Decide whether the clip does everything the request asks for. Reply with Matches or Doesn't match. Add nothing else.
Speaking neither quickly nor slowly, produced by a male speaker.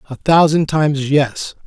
Matches